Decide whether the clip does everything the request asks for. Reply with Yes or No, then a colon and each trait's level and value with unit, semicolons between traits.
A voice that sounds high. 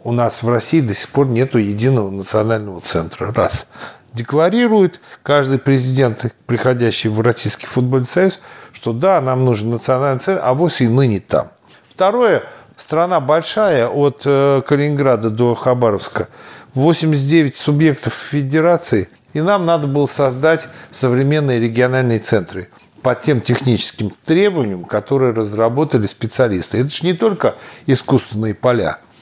No: low, 130 Hz